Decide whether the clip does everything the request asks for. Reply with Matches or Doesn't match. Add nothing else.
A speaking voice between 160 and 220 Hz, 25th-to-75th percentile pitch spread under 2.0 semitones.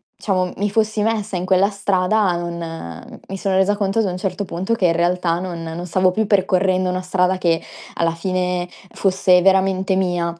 Matches